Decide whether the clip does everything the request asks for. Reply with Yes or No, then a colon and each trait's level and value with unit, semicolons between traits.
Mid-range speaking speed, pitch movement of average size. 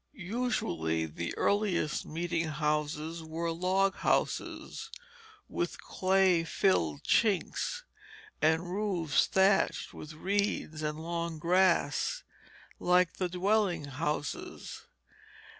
No: slow, 90 wpm; average, 3.8 semitones